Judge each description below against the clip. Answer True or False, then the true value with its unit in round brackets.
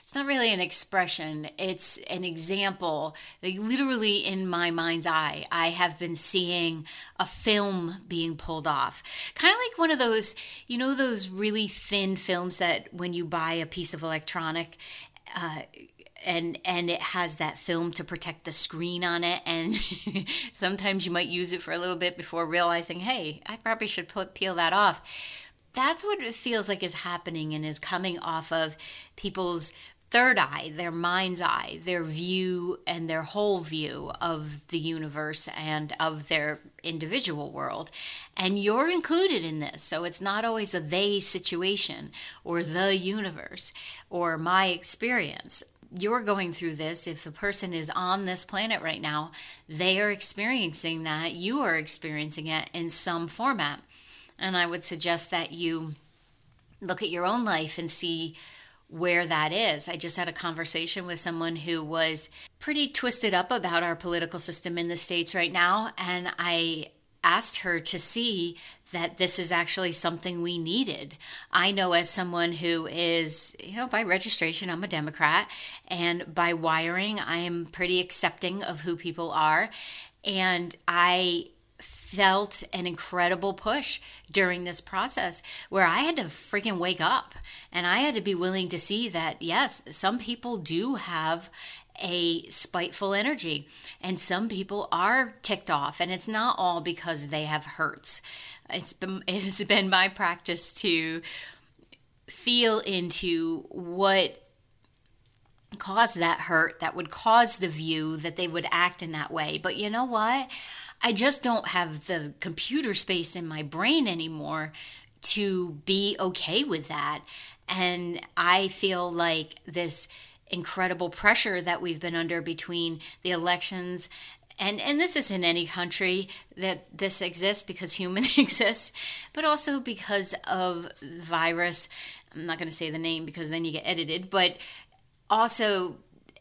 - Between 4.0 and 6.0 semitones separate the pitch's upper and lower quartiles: False (2.7 semitones)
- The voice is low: False (175 Hz)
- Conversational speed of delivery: True (160 wpm)